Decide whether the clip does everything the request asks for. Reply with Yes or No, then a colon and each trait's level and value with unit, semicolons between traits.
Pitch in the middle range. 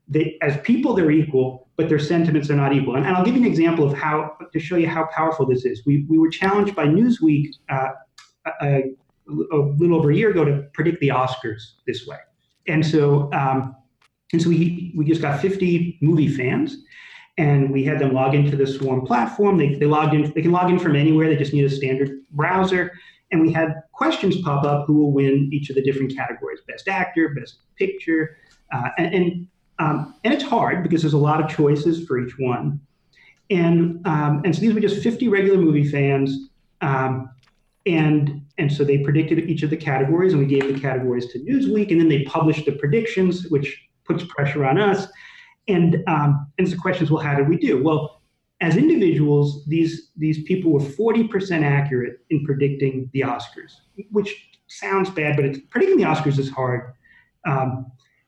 Yes: medium, 155 Hz